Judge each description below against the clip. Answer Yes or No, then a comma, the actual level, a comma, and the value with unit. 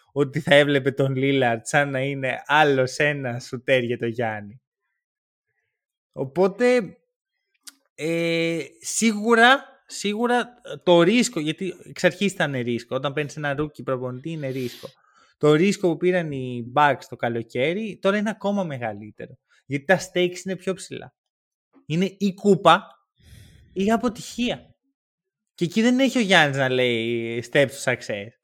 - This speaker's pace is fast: No, average, 140 wpm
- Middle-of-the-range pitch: Yes, medium, 155 Hz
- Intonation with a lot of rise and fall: Yes, wide, 7.0 semitones